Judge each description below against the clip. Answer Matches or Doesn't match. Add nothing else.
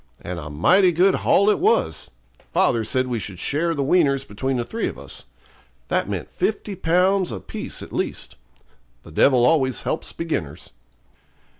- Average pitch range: Doesn't match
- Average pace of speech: Matches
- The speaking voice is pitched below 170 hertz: Matches